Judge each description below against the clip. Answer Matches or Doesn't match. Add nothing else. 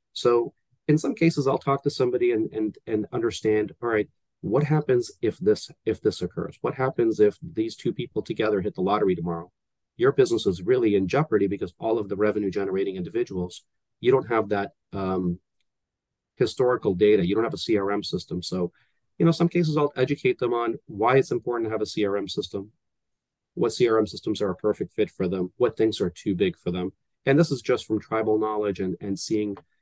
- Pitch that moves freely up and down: Matches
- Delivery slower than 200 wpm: Doesn't match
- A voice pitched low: Matches